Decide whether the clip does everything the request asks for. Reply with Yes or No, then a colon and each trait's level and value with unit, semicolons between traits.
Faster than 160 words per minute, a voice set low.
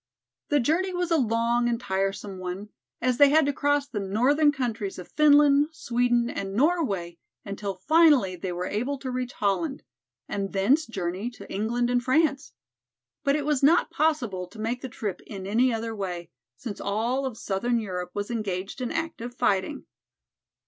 No: average, 170 wpm; high, 235 Hz